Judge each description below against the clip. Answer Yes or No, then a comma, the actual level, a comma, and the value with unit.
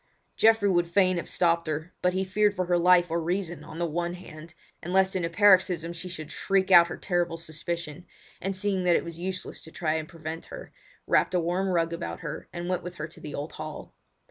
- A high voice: No, medium, 175 Hz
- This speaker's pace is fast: Yes, fast, 230 wpm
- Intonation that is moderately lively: No, narrow, 2.0 semitones